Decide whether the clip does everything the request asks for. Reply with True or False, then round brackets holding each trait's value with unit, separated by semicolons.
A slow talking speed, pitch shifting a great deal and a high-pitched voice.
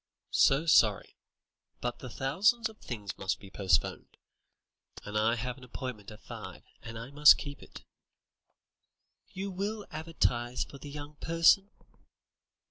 False (130 wpm; 6.4 semitones; 135 Hz)